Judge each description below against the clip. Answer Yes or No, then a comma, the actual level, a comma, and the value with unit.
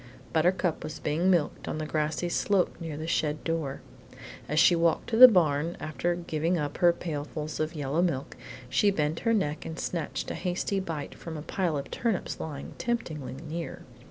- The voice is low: No, medium, 165 Hz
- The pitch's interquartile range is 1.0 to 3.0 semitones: Yes, average, 2.7 semitones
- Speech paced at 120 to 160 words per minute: No, average, 185 wpm